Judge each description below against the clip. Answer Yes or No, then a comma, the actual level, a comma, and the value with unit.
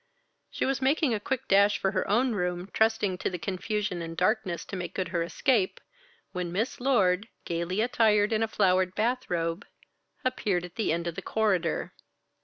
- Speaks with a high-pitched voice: Yes, high, 195 Hz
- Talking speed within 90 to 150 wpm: No, average, 185 wpm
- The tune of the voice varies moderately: Yes, average, 3.8 semitones